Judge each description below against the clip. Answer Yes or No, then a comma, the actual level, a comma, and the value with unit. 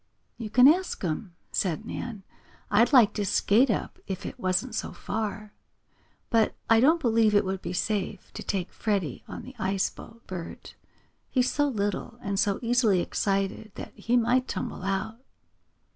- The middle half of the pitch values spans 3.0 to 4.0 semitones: Yes, average, 3.6 semitones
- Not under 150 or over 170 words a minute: Yes, average, 165 wpm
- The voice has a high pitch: Yes, high, 215 Hz